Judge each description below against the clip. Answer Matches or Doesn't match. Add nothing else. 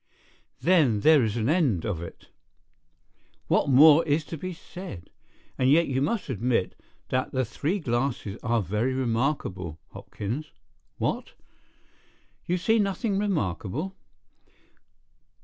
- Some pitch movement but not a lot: Doesn't match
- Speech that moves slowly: Matches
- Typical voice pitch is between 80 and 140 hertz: Matches